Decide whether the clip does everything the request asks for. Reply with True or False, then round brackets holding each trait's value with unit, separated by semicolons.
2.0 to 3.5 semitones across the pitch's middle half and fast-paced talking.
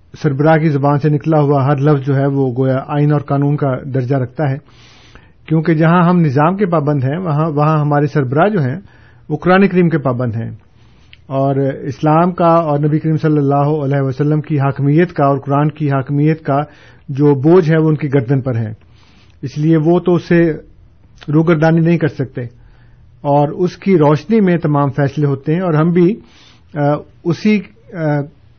False (2.9 semitones; 180 wpm)